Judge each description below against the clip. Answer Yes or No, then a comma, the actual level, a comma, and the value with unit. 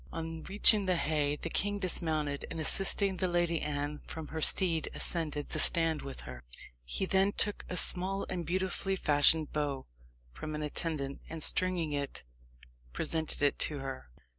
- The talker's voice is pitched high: No, medium, 160 Hz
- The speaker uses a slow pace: No, average, 165 wpm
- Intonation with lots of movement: No, average, 3.8 semitones